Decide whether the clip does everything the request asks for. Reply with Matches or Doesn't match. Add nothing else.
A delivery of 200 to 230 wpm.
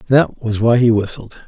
Matches